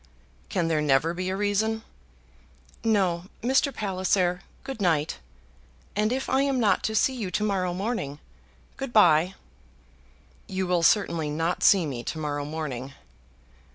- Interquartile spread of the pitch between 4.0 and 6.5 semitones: Yes, average, 5.1 semitones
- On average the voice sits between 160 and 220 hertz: Yes, medium, 185 Hz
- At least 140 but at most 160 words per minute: Yes, average, 145 wpm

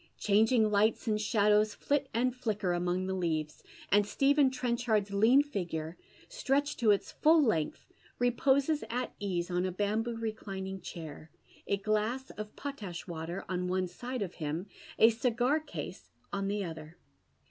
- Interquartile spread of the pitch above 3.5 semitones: Yes, average, 5.1 semitones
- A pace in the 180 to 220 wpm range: No, average, 150 wpm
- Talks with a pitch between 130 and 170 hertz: No, high, 210 Hz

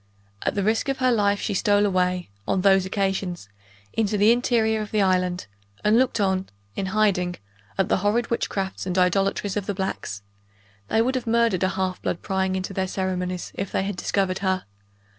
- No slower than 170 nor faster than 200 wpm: Yes, average, 190 wpm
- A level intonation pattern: Yes, narrow, 2.3 semitones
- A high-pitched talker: Yes, high, 195 Hz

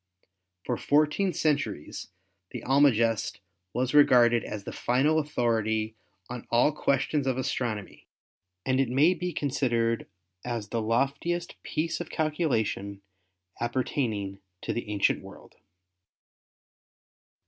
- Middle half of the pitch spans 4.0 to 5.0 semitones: Yes, average, 4.5 semitones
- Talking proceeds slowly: Yes, slow, 115 wpm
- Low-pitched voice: Yes, low, 125 Hz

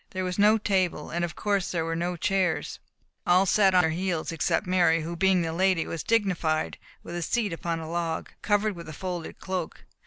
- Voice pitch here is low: No, medium, 175 Hz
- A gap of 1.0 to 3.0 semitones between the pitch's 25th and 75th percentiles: Yes, narrow, 2.6 semitones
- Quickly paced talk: Yes, fast, 210 wpm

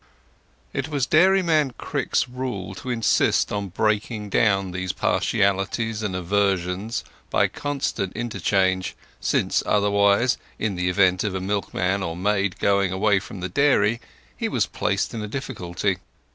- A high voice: No, low, 100 Hz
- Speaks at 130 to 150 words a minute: Yes, average, 140 wpm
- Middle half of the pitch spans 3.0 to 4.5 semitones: Yes, average, 3.4 semitones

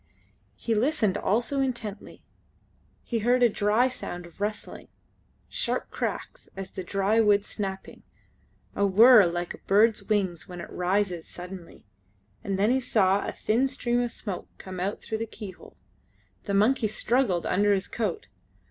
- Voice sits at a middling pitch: No, high, 210 Hz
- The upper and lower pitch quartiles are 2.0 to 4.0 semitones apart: Yes, average, 3.6 semitones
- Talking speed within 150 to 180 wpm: Yes, average, 155 wpm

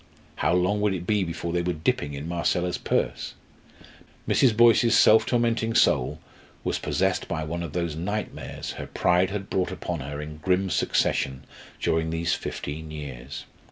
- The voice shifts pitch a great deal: No, average, 4.2 semitones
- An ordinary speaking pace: Yes, average, 160 wpm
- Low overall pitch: Yes, very low, 85 Hz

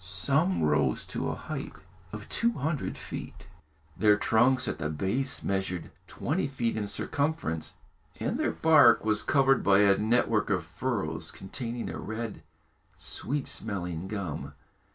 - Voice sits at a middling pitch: No, low, 110 Hz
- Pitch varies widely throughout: Yes, wide, 6.1 semitones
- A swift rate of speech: No, average, 140 wpm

